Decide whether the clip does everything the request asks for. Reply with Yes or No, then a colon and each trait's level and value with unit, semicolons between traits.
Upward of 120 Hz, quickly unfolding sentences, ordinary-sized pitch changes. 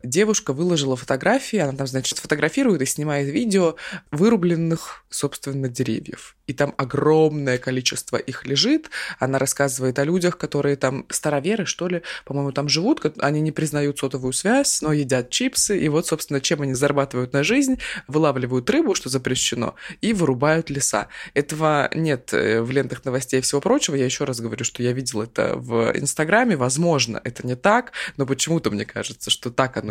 Yes: medium, 140 Hz; fast, 165 wpm; average, 3.7 semitones